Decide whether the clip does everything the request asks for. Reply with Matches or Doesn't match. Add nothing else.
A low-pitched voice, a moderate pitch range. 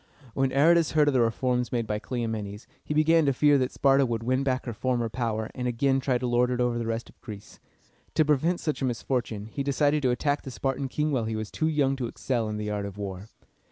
Matches